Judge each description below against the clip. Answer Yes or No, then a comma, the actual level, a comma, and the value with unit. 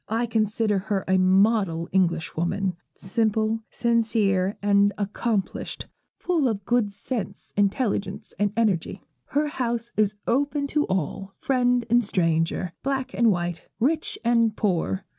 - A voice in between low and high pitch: No, high, 210 Hz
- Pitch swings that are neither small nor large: Yes, average, 3.7 semitones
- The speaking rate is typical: No, slow, 125 wpm